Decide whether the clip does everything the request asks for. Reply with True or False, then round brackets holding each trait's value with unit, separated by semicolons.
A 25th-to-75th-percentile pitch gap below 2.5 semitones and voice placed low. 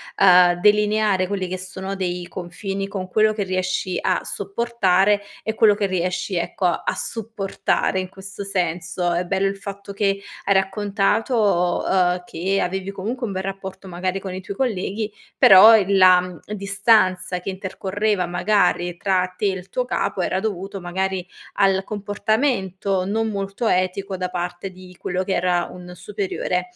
False (1.9 semitones; 190 Hz)